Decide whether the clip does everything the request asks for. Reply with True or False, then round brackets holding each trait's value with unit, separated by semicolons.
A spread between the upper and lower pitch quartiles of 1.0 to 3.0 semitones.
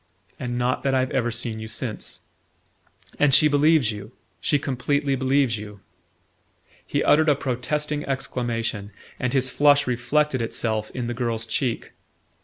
False (3.6 semitones)